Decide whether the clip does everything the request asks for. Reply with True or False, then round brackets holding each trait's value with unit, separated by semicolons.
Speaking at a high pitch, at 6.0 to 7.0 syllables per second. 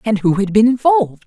True (215 Hz; 6.1 syllables/s)